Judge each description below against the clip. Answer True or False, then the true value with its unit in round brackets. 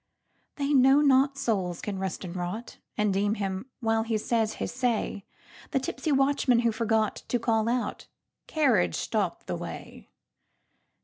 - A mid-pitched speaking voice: False (230 Hz)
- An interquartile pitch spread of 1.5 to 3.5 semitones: False (4.1 semitones)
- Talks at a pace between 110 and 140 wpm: True (135 wpm)